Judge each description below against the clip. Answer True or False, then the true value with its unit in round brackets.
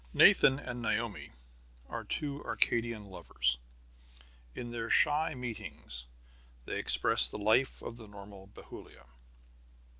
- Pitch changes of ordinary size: True (3.5 semitones)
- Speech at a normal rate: False (115 wpm)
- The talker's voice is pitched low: True (115 Hz)